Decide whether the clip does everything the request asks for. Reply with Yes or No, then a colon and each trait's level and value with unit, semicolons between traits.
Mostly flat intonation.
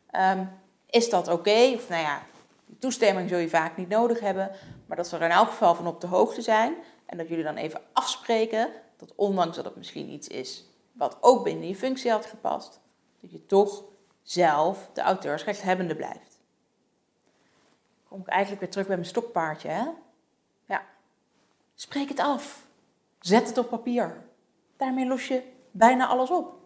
No: average, 5.2 semitones